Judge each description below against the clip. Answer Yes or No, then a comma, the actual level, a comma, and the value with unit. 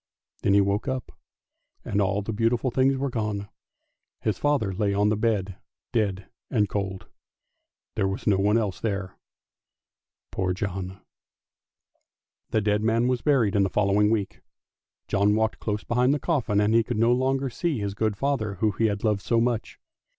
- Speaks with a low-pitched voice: Yes, low, 105 Hz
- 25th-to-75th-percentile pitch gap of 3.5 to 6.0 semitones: No, average, 2.9 semitones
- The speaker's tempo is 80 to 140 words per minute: No, average, 175 wpm